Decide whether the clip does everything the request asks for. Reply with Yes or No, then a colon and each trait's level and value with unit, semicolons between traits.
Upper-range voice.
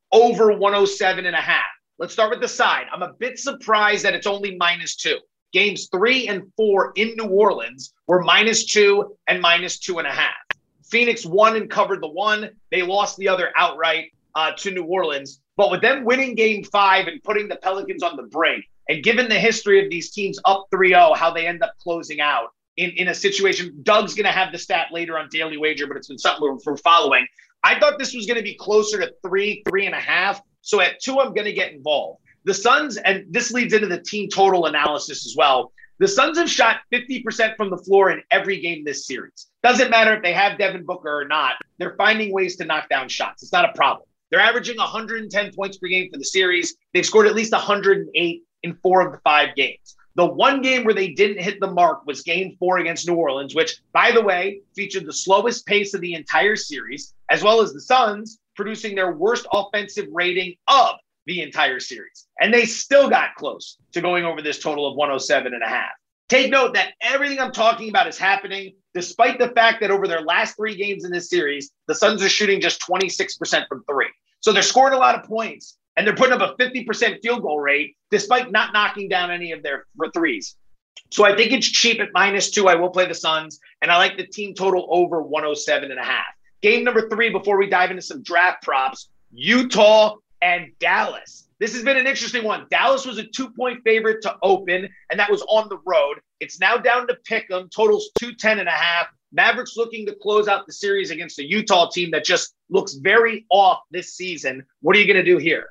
Yes: high, 200 Hz